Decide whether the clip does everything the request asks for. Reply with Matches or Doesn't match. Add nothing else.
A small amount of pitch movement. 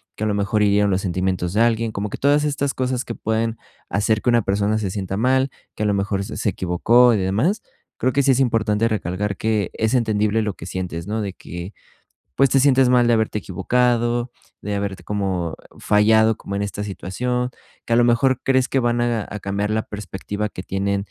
Doesn't match